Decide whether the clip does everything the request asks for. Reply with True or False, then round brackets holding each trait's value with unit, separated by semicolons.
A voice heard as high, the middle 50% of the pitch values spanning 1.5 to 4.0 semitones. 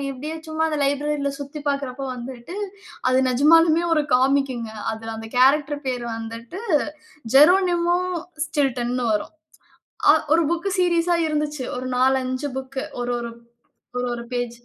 True (275 Hz; 3.7 semitones)